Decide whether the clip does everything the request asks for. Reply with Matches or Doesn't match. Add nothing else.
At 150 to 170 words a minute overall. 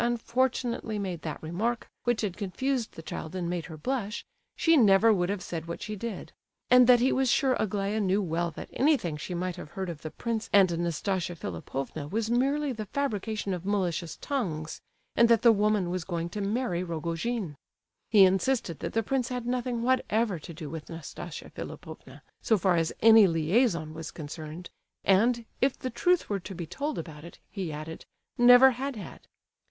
Doesn't match